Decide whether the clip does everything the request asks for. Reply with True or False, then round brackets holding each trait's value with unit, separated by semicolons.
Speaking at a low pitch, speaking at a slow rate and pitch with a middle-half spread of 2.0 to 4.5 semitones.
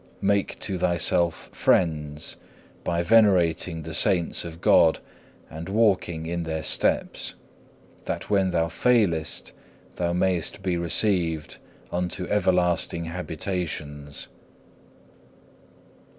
True (85 Hz; 95 wpm; 2.5 semitones)